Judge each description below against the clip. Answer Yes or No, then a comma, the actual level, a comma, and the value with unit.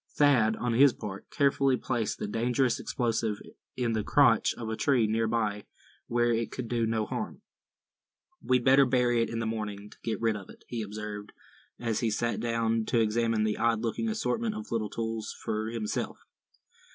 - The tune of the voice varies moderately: No, narrow, 1.9 semitones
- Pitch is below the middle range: Yes, low, 115 Hz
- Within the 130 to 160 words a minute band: No, average, 185 wpm